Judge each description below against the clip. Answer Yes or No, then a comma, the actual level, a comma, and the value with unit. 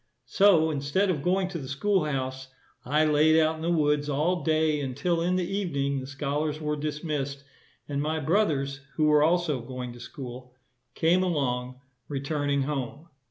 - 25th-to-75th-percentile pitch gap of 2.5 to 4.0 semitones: Yes, average, 2.8 semitones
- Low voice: No, medium, 150 Hz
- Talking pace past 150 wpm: Yes, average, 165 wpm